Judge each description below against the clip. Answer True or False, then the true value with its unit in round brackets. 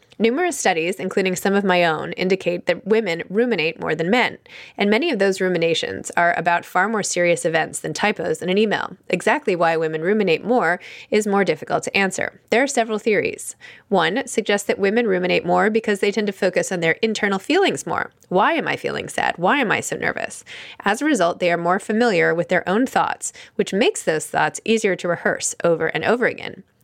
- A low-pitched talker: False (195 Hz)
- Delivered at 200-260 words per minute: True (205 wpm)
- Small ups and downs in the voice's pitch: False (4.3 semitones)